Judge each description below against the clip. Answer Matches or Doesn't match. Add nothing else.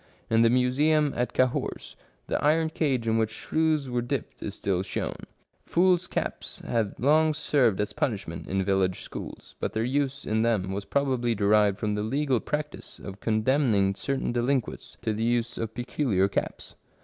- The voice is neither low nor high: Doesn't match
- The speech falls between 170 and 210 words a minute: Matches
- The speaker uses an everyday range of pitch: Matches